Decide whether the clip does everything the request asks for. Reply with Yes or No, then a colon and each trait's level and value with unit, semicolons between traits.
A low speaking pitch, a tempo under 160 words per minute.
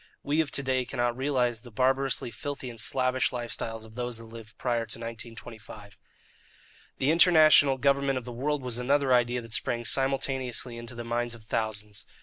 No: low, 125 Hz; average, 175 wpm